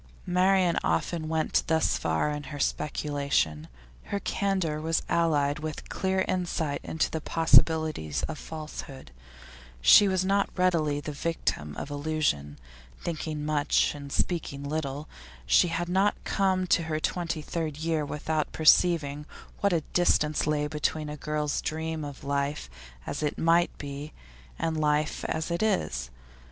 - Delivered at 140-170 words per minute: Yes, average, 145 wpm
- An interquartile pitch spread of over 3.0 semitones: No, average, 2.7 semitones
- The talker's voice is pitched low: No, medium, 155 Hz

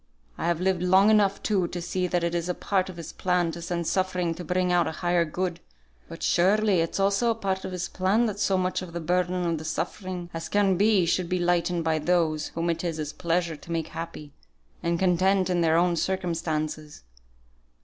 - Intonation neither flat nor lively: No, narrow, 2.0 semitones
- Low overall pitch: No, medium, 175 Hz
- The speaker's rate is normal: No, fast, 210 wpm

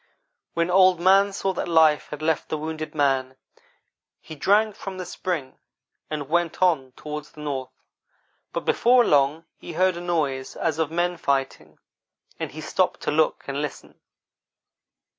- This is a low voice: No, medium, 160 Hz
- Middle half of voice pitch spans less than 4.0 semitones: Yes, average, 3.6 semitones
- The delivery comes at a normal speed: Yes, average, 160 wpm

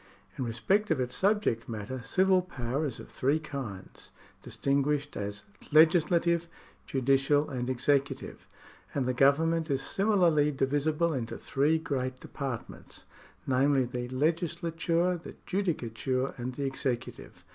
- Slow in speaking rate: Yes, slow, 125 wpm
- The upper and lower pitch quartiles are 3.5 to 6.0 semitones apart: Yes, average, 4.3 semitones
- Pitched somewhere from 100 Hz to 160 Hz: Yes, medium, 140 Hz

